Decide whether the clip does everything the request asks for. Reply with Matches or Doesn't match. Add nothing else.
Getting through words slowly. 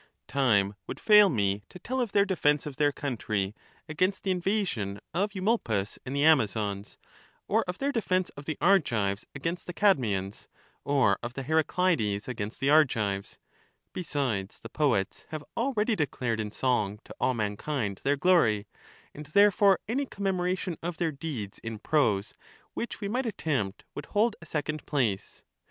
Doesn't match